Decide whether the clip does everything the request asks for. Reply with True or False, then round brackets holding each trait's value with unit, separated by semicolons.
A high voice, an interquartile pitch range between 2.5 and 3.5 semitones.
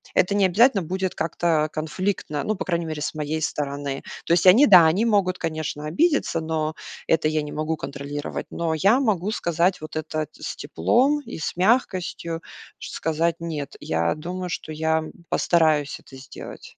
False (165 Hz; 3.2 semitones)